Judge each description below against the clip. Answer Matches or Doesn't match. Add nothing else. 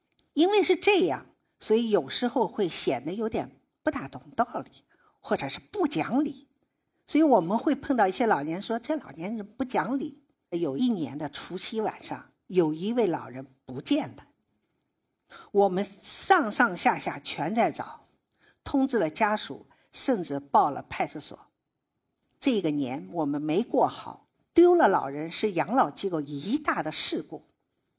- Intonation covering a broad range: Matches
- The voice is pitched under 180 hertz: Doesn't match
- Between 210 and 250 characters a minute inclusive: Matches